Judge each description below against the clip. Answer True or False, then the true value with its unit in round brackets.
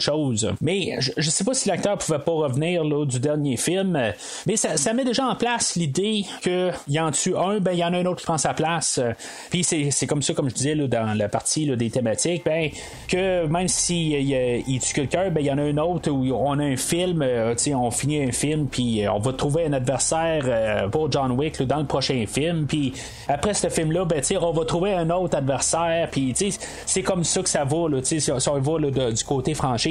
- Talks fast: True (250 wpm)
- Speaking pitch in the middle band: True (155 Hz)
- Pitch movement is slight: False (4.3 semitones)